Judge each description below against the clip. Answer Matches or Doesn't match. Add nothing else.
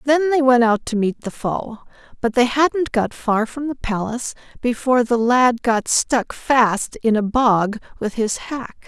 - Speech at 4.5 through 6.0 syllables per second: Doesn't match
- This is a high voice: Matches